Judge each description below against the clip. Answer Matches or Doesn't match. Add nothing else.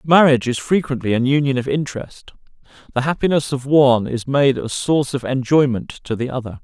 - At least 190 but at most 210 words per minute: Doesn't match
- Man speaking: Matches